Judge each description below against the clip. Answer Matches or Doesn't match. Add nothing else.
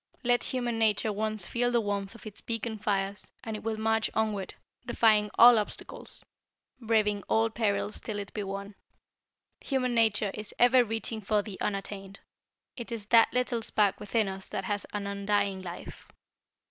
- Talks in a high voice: Matches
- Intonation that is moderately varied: Doesn't match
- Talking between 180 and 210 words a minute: Doesn't match